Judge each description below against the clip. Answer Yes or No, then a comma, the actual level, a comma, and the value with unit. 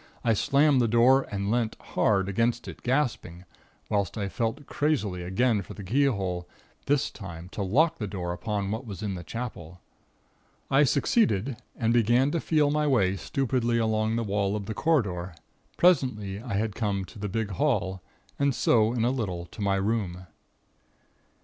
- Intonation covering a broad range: No, average, 4.7 semitones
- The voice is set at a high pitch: No, low, 110 Hz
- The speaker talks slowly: No, average, 170 wpm